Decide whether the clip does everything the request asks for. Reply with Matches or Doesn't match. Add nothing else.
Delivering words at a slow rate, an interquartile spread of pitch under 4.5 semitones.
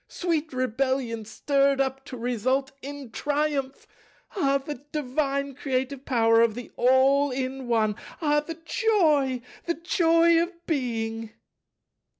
Matches